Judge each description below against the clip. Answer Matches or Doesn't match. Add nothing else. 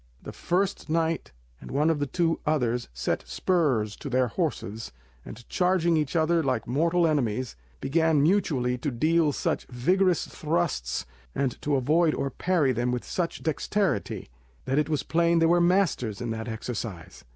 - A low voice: Doesn't match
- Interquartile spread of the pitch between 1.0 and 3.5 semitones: Doesn't match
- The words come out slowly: Doesn't match